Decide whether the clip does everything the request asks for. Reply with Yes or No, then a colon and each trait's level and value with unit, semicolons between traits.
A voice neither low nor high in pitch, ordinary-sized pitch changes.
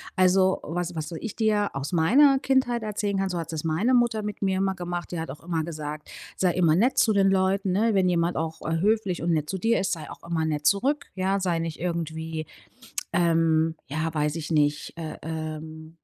Yes: medium, 175 Hz; average, 3.5 semitones